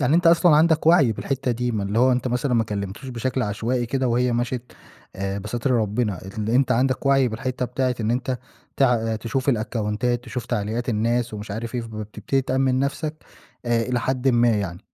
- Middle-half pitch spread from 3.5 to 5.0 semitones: No, average, 2.8 semitones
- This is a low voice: Yes, low, 120 Hz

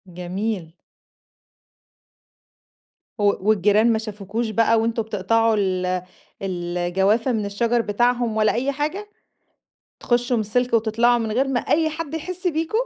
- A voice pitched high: Yes, high, 225 Hz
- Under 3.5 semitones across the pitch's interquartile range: Yes, average, 3.1 semitones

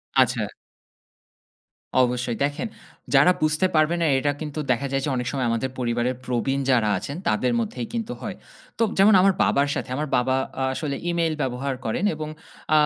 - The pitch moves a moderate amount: Yes, average, 3.8 semitones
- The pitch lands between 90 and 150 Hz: Yes, low, 135 Hz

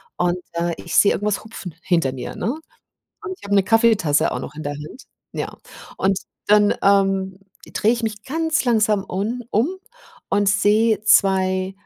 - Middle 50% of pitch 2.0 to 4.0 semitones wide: Yes, average, 2.9 semitones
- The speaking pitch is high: Yes, high, 200 Hz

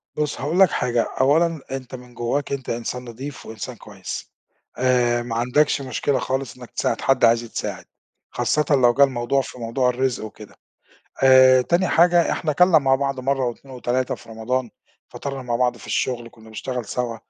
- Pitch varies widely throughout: No, narrow, 2.5 semitones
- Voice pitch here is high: No, low, 130 Hz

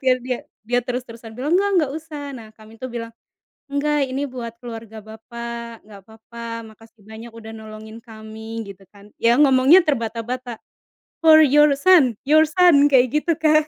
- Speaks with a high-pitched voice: Yes, high, 240 Hz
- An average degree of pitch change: Yes, average, 4.3 semitones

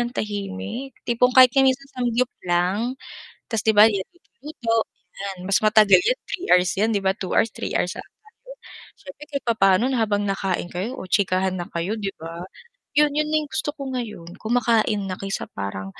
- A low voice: No, high, 215 Hz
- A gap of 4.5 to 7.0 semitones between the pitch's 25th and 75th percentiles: Yes, average, 5.1 semitones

